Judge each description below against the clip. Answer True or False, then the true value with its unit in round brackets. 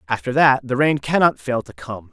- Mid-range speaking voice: False (130 Hz)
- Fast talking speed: True (225 wpm)